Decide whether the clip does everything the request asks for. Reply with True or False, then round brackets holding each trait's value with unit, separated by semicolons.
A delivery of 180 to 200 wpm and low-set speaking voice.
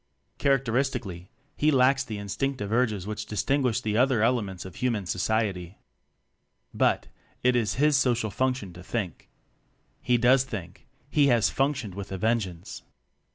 False (140 wpm; 115 Hz)